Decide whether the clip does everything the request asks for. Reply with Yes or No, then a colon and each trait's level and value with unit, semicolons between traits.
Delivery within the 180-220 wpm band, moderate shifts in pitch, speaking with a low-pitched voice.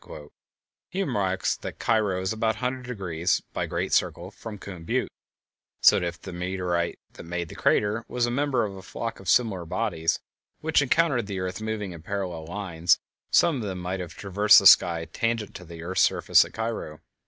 Yes: average, 190 wpm; average, 4.3 semitones; very low, 95 Hz